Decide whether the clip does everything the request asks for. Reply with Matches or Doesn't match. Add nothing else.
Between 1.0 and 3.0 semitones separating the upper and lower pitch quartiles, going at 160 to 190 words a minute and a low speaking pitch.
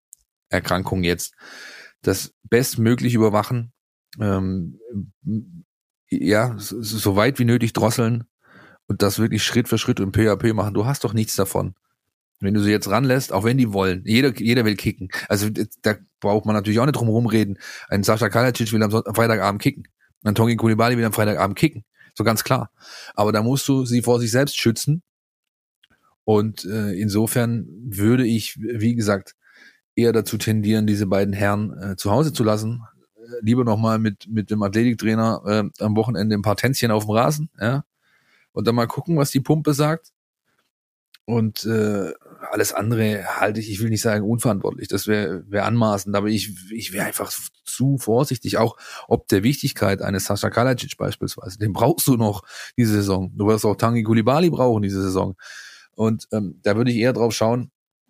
Matches